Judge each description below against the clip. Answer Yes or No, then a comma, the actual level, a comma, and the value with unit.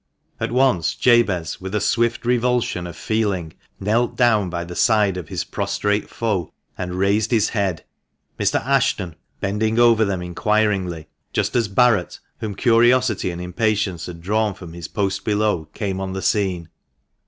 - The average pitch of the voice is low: Yes, low, 105 Hz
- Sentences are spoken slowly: No, average, 155 wpm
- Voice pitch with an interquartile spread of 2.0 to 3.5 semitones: No, average, 4.1 semitones